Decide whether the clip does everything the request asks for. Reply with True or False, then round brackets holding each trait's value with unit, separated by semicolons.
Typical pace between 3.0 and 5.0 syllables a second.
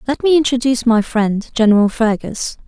False (5.4 syllables/s)